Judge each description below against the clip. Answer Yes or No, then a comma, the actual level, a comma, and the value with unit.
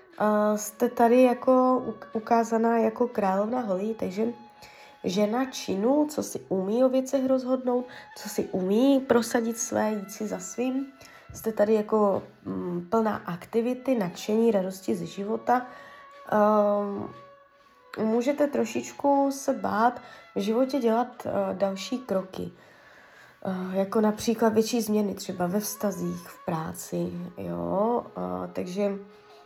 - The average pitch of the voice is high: Yes, high, 220 Hz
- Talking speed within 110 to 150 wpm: Yes, average, 120 wpm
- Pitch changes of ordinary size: Yes, average, 4.3 semitones